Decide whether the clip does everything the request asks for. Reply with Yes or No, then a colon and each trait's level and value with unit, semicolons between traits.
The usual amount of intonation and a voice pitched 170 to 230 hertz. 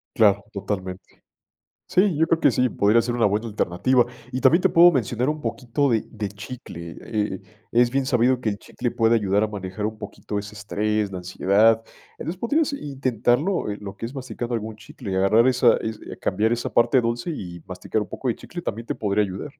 No: average, 3.8 semitones; low, 115 Hz